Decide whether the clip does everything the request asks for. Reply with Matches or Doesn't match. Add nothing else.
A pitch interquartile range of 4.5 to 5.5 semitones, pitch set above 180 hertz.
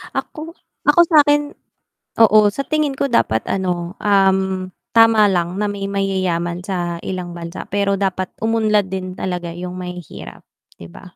Doesn't match